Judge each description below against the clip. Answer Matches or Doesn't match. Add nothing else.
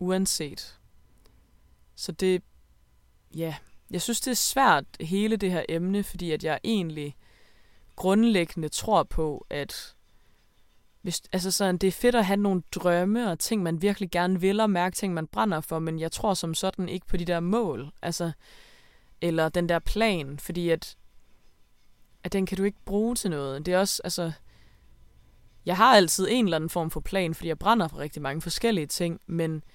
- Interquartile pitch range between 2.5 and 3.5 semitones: Doesn't match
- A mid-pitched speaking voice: Matches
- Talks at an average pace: Matches